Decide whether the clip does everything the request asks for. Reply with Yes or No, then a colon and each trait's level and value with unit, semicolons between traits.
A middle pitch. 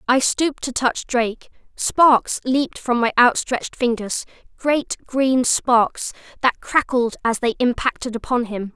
No: very high, 250 Hz